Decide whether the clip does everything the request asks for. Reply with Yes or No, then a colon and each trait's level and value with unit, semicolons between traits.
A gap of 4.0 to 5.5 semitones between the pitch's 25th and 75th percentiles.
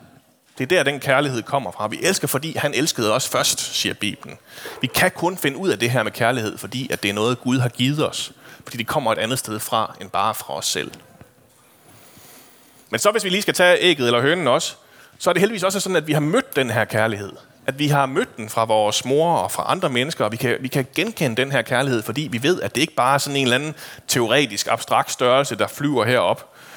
Yes: average, 4.5 semitones